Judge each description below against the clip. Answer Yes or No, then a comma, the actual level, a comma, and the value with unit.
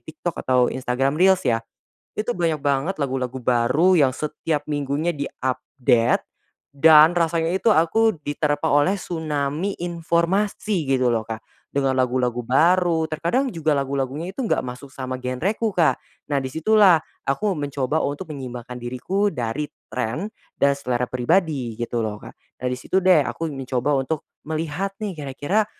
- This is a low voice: No, medium, 145 Hz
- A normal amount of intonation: Yes, average, 4.9 semitones